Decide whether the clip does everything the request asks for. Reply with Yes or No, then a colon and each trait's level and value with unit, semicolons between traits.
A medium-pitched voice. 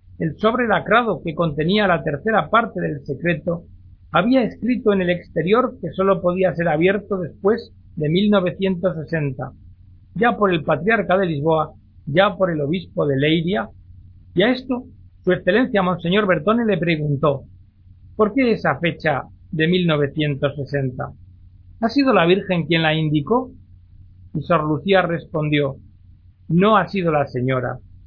Yes: medium, 165 Hz